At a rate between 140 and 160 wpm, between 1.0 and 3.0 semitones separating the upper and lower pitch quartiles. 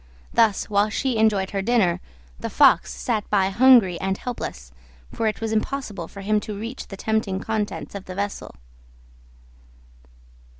Yes: average, 155 wpm; narrow, 2.5 semitones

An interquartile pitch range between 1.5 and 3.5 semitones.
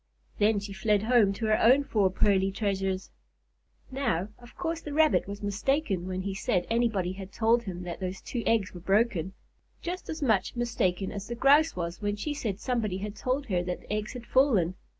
No: average, 4.0 semitones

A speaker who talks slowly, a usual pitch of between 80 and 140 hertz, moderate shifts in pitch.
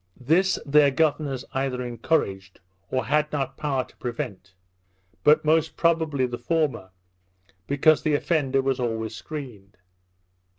Yes: slow, 125 wpm; low, 135 Hz; average, 3.8 semitones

